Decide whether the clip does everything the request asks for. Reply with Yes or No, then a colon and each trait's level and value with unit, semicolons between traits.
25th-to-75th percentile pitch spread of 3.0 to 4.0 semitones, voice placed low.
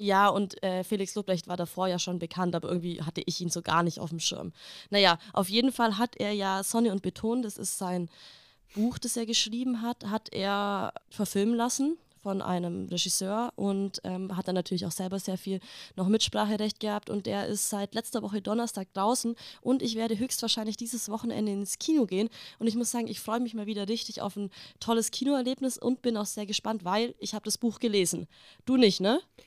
No: average, 3.5 semitones; high, 210 Hz